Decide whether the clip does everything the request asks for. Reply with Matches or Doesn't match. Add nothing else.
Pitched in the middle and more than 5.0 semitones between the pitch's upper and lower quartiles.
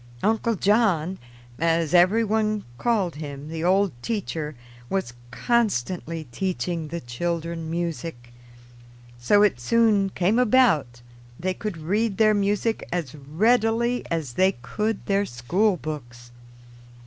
Matches